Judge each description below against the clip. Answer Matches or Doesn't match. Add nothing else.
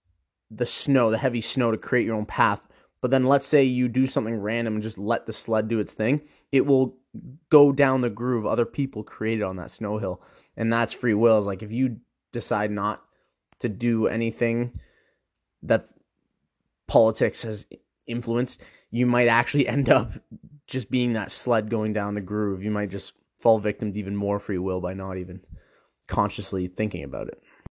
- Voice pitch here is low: Matches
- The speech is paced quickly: Doesn't match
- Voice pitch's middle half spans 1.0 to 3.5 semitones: Matches